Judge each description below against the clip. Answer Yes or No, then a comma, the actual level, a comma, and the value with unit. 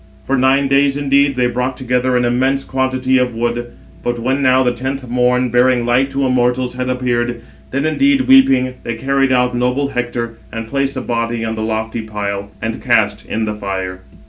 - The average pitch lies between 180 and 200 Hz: No, low, 125 Hz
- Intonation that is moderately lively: No, narrow, 2.0 semitones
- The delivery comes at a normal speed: Yes, average, 190 wpm